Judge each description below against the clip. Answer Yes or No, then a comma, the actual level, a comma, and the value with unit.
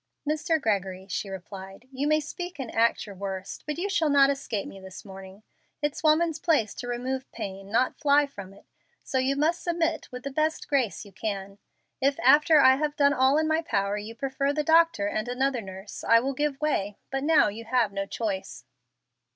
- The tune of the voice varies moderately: No, wide, 6.7 semitones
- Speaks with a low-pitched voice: No, very high, 260 Hz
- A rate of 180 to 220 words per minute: Yes, average, 200 wpm